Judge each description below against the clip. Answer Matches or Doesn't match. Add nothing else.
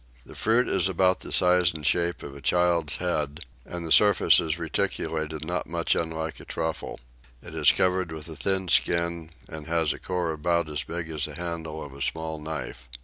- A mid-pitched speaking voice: Doesn't match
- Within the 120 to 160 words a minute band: Doesn't match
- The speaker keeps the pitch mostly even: Matches